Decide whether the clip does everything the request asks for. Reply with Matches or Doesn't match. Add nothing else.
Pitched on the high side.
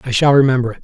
Doesn't match